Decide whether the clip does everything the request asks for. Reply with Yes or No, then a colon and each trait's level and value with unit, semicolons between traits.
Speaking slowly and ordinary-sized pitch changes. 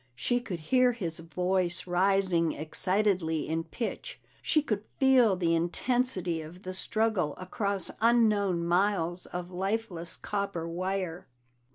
Yes: slow, 125 wpm; average, 3.9 semitones